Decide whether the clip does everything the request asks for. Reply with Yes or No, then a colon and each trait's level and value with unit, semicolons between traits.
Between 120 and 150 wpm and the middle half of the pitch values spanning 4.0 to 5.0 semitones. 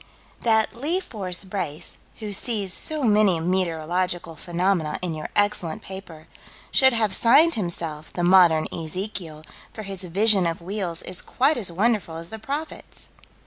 Yes: average, 145 wpm; average, 4.4 semitones